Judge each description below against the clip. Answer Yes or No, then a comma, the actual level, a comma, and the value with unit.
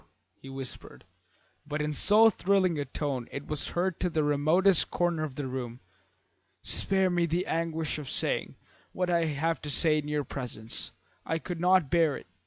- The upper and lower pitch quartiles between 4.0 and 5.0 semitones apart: No, average, 3.5 semitones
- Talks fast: No, average, 180 wpm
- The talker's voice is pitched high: No, medium, 155 Hz